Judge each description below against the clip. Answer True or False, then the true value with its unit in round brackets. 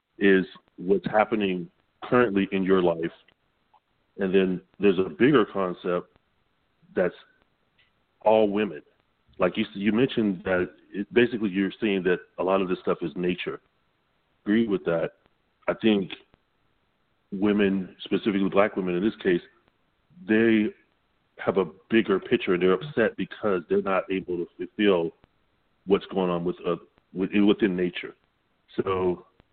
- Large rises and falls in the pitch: False (2.8 semitones)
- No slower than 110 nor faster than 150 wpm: True (140 wpm)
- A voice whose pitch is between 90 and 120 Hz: True (95 Hz)